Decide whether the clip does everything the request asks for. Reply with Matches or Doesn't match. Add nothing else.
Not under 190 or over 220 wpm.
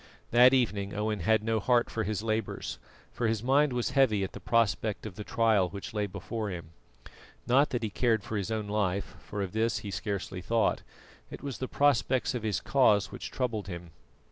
Matches